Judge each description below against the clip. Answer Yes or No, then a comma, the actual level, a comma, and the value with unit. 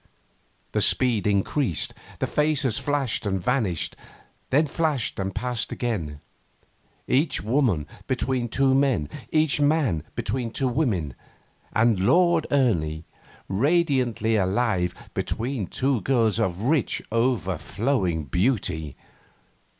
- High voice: No, low, 120 Hz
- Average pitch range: No, wide, 6.3 semitones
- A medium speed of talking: No, slow, 105 wpm